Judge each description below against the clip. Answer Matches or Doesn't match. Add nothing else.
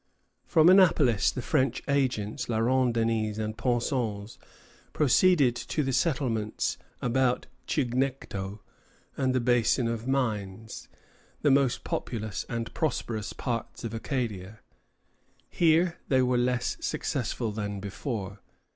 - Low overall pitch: Matches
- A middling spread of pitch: Matches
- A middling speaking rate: Doesn't match